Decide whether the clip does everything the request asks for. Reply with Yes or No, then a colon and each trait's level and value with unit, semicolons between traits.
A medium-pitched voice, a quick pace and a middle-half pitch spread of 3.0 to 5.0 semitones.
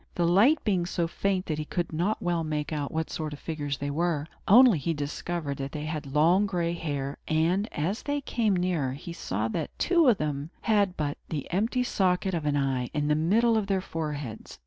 Yes: medium, 165 Hz; fast, 210 wpm; average, 4.5 semitones